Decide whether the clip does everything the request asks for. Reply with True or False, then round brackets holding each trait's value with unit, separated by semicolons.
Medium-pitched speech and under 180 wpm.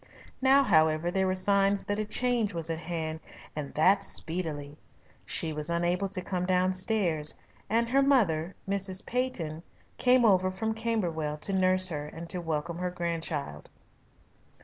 True (180 Hz; 150 wpm)